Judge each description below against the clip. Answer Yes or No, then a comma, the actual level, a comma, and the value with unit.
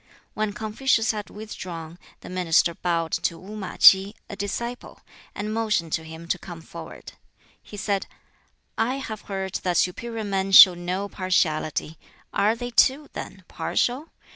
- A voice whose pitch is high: Yes, high, 195 Hz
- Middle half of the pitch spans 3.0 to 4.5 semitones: Yes, average, 3.7 semitones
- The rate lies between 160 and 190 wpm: No, average, 150 wpm